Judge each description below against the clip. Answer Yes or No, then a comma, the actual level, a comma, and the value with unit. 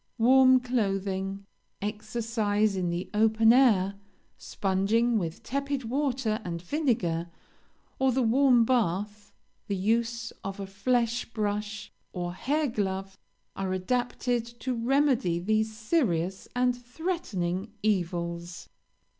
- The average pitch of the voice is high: Yes, high, 215 Hz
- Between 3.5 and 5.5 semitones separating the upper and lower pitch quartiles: Yes, average, 4.4 semitones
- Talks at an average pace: No, slow, 110 wpm